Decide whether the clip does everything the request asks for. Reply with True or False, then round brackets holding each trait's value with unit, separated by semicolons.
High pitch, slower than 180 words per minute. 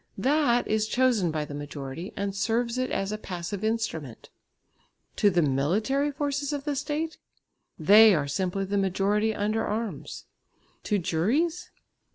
True (210 Hz; 145 wpm)